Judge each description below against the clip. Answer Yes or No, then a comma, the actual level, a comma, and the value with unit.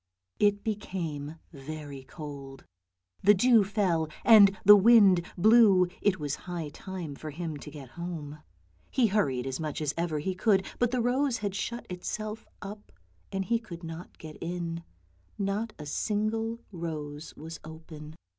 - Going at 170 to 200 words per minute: No, average, 155 wpm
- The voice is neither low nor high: Yes, medium, 175 Hz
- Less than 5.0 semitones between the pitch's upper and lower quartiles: No, average, 5.3 semitones